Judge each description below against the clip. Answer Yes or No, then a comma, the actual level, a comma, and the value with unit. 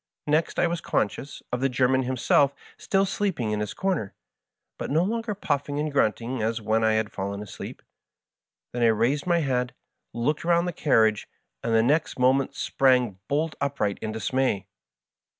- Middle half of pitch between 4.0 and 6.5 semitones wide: Yes, wide, 5.4 semitones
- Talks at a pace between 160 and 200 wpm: Yes, average, 170 wpm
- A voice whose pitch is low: Yes, low, 130 Hz